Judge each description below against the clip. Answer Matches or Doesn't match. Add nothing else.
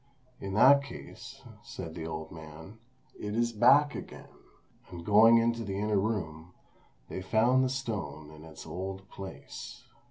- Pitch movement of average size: Doesn't match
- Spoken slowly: Doesn't match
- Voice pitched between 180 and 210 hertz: Doesn't match